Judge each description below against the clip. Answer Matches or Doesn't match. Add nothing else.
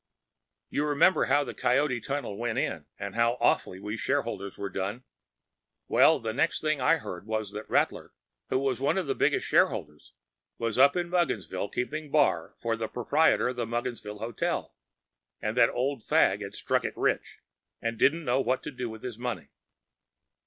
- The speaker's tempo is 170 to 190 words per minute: Matches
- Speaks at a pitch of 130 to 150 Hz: Doesn't match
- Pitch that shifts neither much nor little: Matches